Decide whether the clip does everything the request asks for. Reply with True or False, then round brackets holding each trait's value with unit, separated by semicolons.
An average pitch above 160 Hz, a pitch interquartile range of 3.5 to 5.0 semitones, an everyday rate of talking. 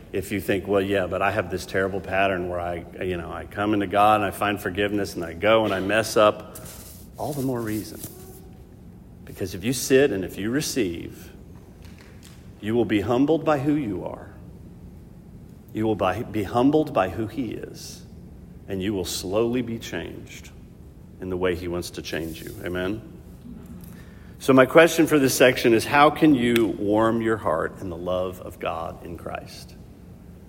False (100 Hz; 4.1 semitones; 185 wpm)